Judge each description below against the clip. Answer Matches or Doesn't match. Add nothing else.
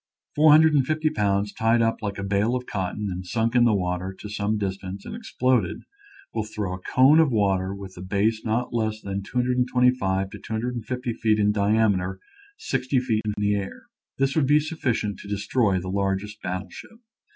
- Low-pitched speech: Matches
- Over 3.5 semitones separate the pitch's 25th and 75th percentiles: Matches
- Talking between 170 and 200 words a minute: Matches